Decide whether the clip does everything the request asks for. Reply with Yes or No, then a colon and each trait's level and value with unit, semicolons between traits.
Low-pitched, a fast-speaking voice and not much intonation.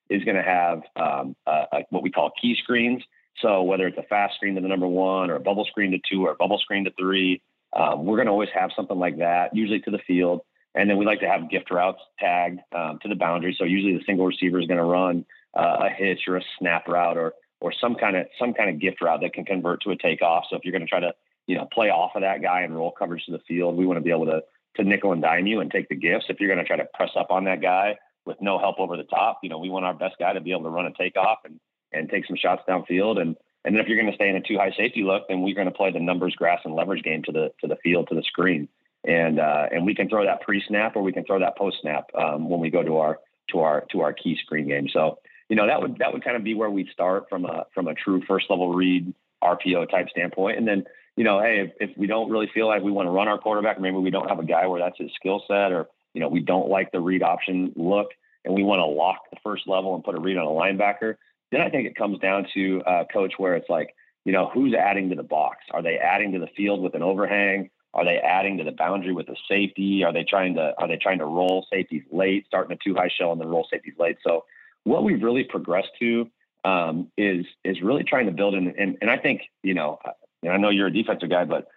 Yes: very low, 95 Hz; fast, 285 wpm; narrow, 2.0 semitones